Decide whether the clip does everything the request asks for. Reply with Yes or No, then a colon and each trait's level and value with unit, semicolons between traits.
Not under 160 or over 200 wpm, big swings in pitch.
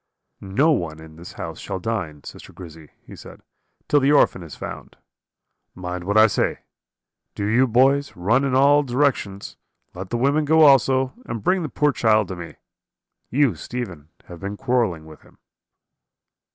Yes: average, 165 wpm; wide, 7.4 semitones